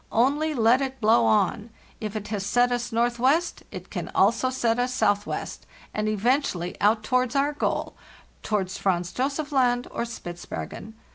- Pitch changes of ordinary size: Yes, average, 3.5 semitones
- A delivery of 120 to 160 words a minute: Yes, average, 150 wpm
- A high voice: Yes, high, 235 Hz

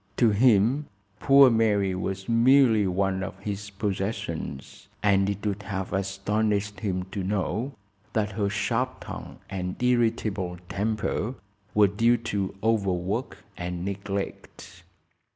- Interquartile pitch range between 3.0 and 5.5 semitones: No, narrow, 2.6 semitones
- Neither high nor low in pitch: No, low, 100 Hz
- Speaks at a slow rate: Yes, slow, 120 wpm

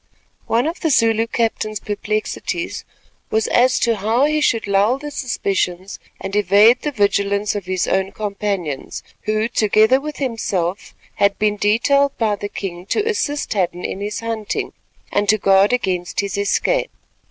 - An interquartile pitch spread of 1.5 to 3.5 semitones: Yes, average, 3.2 semitones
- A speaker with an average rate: Yes, average, 155 wpm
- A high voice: Yes, high, 210 Hz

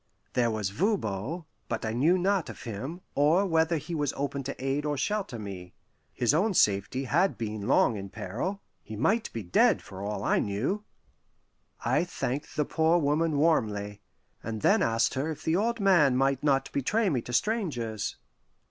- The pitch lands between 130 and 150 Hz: Yes, medium, 140 Hz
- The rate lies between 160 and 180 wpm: Yes, average, 175 wpm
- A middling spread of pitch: No, wide, 7.2 semitones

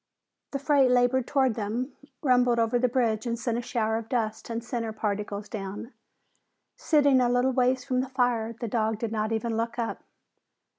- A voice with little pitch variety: Yes, narrow, 2.3 semitones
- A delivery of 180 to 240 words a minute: Yes, average, 185 wpm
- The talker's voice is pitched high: Yes, high, 235 Hz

